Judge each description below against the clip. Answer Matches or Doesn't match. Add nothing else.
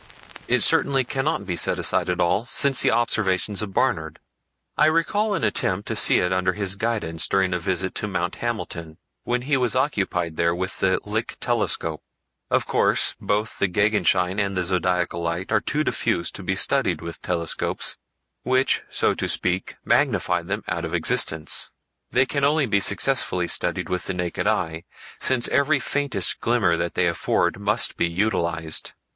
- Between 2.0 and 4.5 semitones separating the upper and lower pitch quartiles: Doesn't match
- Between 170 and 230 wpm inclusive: Matches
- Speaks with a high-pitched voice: Doesn't match